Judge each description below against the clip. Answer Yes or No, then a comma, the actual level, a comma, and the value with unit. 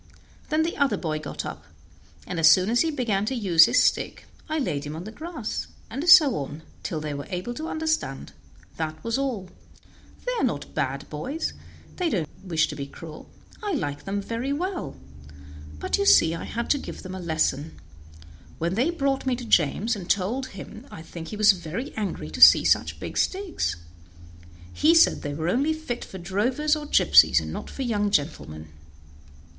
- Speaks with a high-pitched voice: Yes, high, 210 Hz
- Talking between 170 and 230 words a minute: Yes, average, 195 wpm